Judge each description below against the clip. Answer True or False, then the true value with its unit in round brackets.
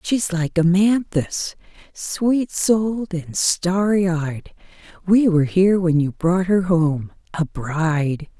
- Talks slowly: True (120 wpm)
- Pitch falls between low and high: True (175 Hz)